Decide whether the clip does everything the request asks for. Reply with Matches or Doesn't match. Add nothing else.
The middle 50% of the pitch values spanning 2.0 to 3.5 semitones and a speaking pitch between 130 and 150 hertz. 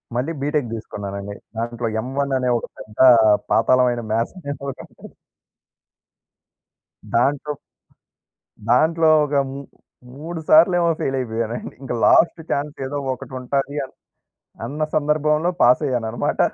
Doesn't match